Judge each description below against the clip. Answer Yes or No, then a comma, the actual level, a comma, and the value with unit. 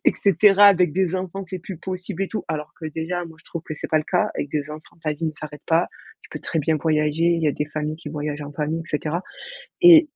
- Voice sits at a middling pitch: Yes, medium, 160 Hz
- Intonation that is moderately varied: Yes, average, 3.2 semitones